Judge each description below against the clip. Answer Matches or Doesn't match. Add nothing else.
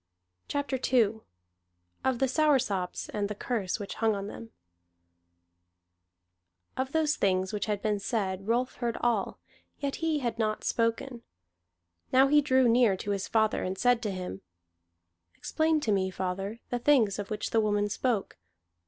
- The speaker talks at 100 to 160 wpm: Matches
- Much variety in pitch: Doesn't match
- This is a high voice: Matches